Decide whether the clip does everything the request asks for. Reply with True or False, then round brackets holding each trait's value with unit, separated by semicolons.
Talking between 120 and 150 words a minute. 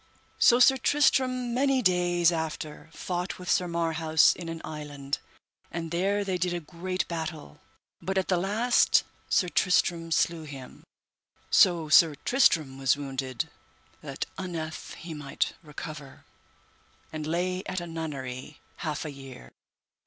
True (140 wpm)